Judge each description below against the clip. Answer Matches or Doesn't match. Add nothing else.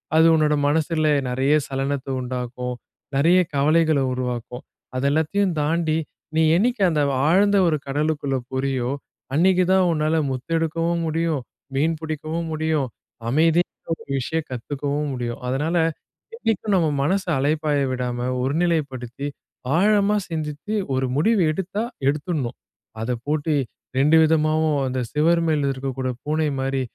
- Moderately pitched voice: Matches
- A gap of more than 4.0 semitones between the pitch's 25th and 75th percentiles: Doesn't match